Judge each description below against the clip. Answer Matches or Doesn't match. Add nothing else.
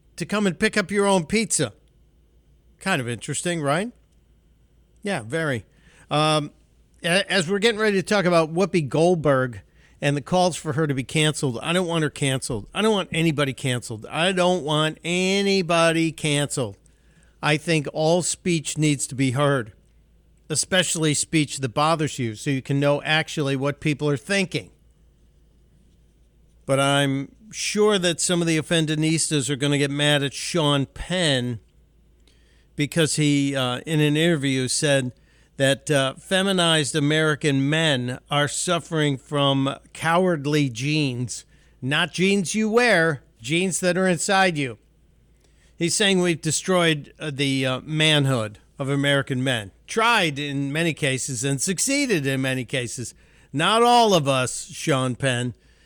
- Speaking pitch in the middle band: Matches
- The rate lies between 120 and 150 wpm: Matches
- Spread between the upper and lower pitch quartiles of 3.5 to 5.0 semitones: Matches